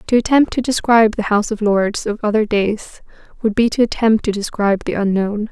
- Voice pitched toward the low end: No, high, 215 Hz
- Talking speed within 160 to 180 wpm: No, fast, 205 wpm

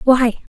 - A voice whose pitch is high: Yes, very high, 250 Hz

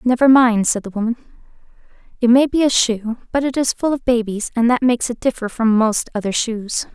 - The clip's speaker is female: Yes, female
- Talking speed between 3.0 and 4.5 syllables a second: No, 5.6 syllables/s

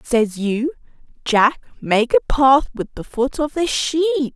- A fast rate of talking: No, average, 165 wpm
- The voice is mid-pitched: No, very high, 265 Hz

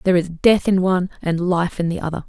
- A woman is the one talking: Yes, female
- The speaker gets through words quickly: Yes, fast, 265 wpm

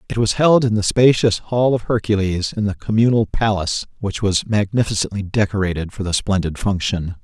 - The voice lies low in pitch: Yes, low, 105 Hz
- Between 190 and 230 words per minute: No, average, 175 wpm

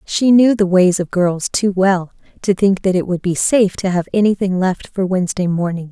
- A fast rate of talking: Yes, fast, 225 wpm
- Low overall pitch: No, high, 190 Hz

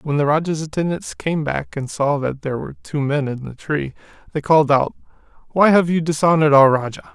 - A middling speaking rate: No, fast, 210 wpm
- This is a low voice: No, medium, 150 Hz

